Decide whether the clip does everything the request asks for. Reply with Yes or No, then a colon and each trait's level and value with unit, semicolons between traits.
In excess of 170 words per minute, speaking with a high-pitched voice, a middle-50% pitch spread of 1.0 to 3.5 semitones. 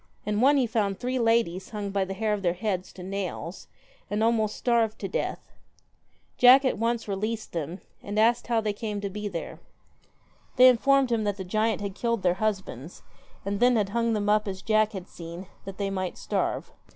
Yes: average, 200 wpm; high, 210 Hz; average, 3.1 semitones